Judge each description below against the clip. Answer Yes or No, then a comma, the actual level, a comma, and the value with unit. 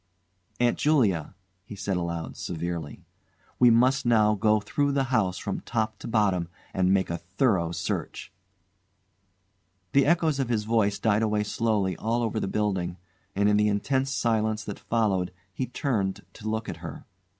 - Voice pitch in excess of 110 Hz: No, low, 105 Hz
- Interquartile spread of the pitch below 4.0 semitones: Yes, average, 3.6 semitones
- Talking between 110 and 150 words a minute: No, average, 160 wpm